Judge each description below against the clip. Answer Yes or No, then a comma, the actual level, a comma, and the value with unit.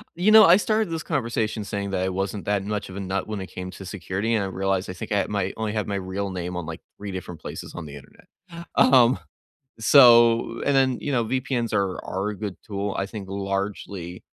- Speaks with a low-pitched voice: Yes, low, 100 Hz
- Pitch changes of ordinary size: Yes, average, 3.5 semitones